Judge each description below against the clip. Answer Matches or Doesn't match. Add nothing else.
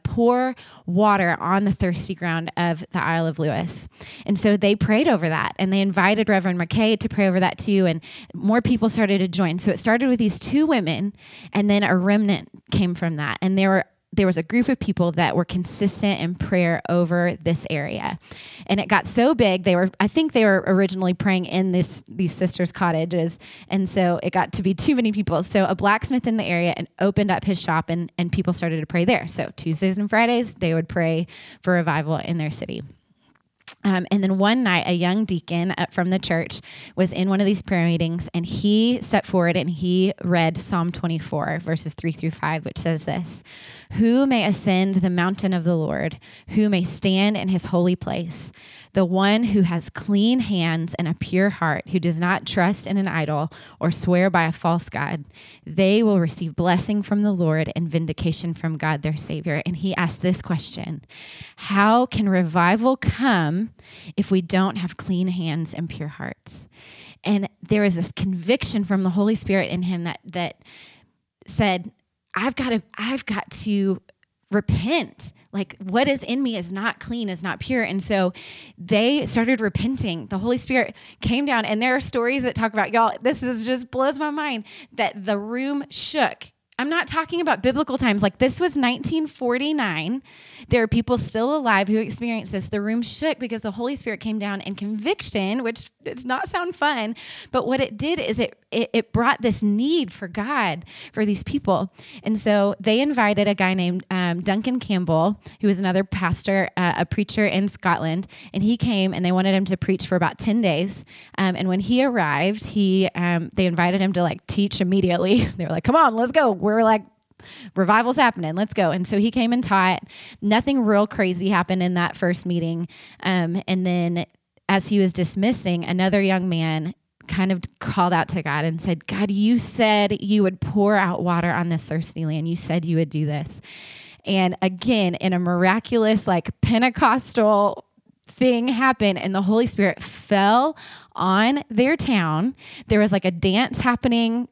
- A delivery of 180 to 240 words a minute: Matches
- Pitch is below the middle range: Doesn't match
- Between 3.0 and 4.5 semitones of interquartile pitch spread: Matches